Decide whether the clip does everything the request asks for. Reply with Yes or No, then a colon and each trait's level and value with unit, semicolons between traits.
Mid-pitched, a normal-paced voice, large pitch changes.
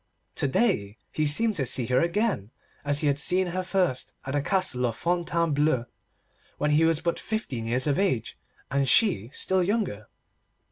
Yes: medium, 150 Hz; average, 175 wpm; wide, 6.1 semitones